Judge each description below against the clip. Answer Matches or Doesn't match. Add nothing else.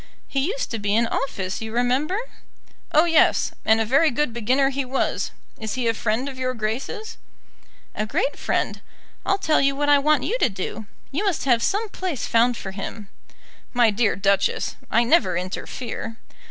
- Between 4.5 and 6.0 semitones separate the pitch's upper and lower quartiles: Matches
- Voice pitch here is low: Doesn't match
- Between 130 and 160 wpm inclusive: Doesn't match